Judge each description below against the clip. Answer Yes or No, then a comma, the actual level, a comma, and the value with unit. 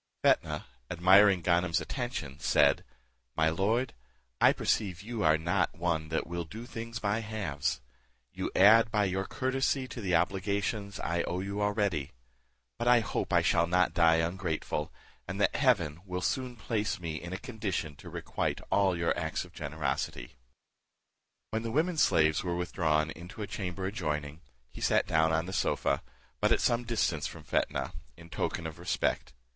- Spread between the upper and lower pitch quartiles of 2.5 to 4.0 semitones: No, average, 4.9 semitones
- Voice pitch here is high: No, very low, 90 Hz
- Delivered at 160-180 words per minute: Yes, average, 165 wpm